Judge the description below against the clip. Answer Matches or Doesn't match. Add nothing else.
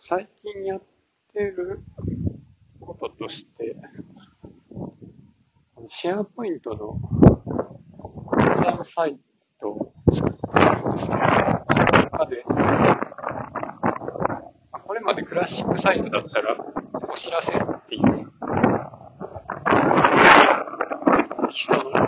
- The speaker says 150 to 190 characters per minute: Matches